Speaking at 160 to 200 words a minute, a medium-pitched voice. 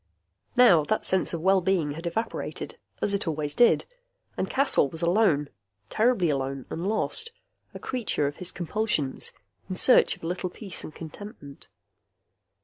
No: average, 150 wpm; medium, 180 Hz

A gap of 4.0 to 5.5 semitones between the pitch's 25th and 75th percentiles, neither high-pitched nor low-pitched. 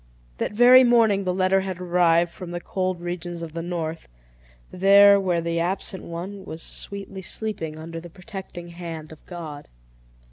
No: narrow, 2.5 semitones; medium, 175 Hz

